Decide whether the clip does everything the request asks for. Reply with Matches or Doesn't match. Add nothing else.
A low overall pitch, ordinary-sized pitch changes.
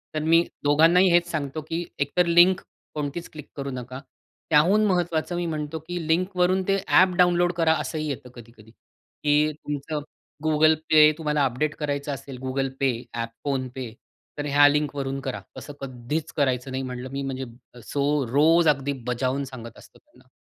Doesn't match